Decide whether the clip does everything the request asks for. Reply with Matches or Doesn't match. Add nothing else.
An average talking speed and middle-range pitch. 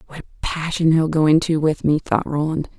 Doesn't match